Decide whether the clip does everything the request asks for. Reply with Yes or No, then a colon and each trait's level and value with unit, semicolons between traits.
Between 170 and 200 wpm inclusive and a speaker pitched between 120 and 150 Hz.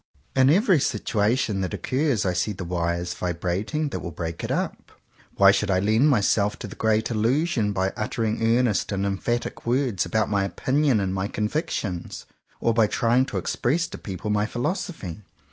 No: average, 180 wpm; low, 110 Hz